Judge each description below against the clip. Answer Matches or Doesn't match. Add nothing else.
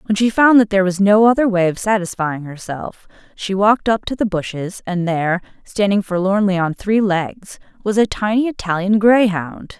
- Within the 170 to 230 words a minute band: Matches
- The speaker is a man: Doesn't match